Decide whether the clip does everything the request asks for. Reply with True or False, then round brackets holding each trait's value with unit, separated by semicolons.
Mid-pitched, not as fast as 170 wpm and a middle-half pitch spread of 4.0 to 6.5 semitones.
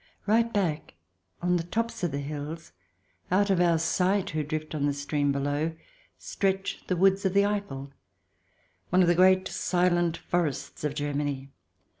True (170 Hz; 160 wpm; 4.4 semitones)